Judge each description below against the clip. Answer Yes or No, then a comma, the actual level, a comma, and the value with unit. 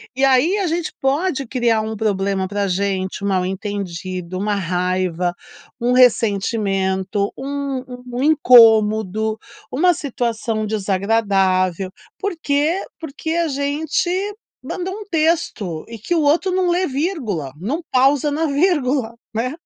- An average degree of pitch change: No, wide, 6.9 semitones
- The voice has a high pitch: Yes, high, 230 Hz